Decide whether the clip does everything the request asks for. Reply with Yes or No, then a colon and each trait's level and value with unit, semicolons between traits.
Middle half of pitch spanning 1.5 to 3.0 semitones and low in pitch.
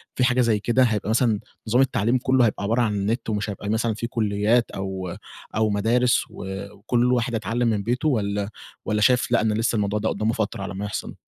Yes: average, 2.7 semitones; low, 110 Hz